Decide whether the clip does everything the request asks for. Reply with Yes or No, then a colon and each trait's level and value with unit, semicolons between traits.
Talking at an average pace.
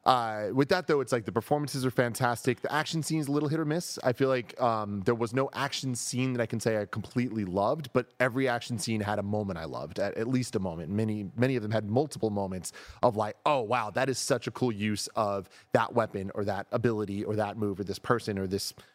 No: fast, 245 wpm